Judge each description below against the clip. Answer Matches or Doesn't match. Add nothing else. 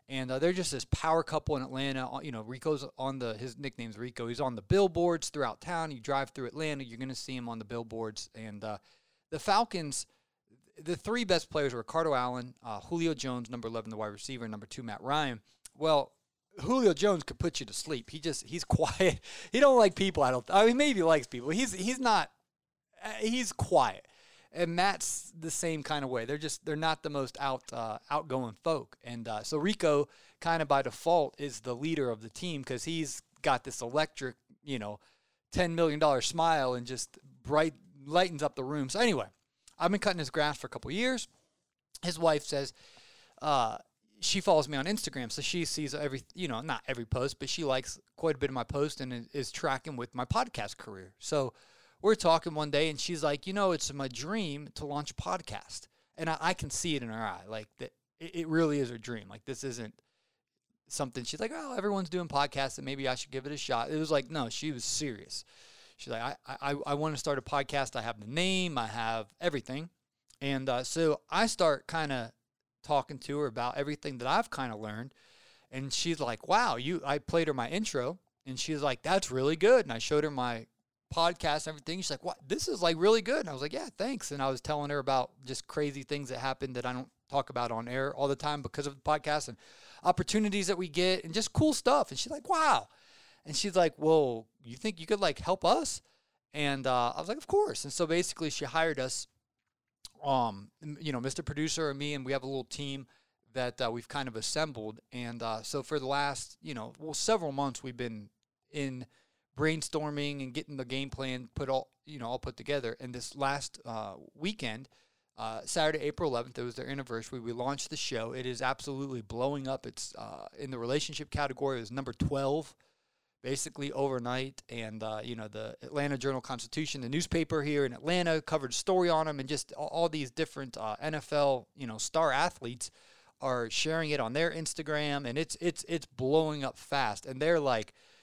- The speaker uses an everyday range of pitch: Matches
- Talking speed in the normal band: Doesn't match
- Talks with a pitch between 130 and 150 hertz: Matches